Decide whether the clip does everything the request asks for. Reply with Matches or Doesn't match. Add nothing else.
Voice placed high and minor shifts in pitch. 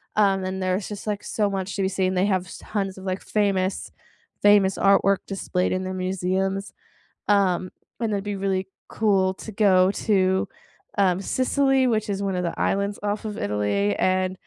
Matches